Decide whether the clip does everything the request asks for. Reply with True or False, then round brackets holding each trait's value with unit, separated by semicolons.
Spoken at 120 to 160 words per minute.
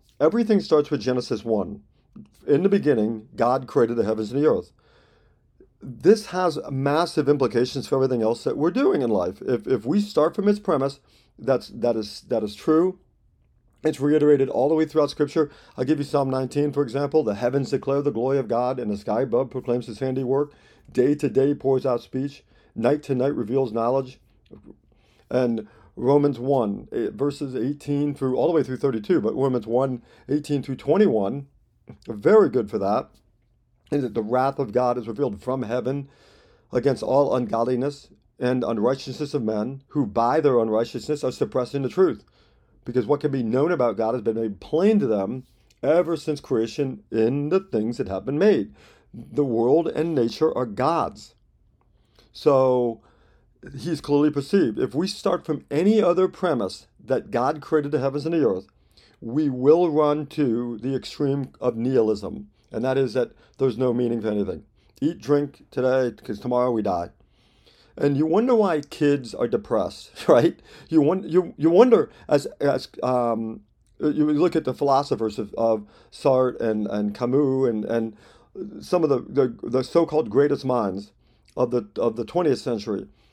False (175 wpm)